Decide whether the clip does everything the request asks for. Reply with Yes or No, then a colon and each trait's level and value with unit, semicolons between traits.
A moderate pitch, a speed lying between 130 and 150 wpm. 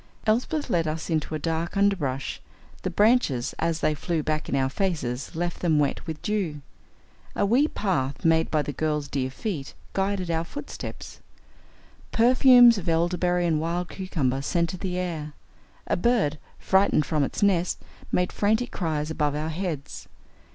No: medium, 165 Hz; average, 160 wpm